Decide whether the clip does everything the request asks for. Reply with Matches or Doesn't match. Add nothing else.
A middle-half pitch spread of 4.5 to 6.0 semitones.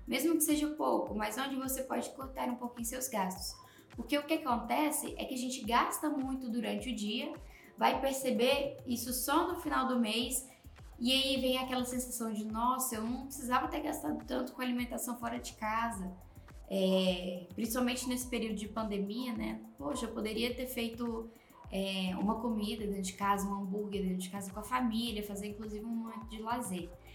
Doesn't match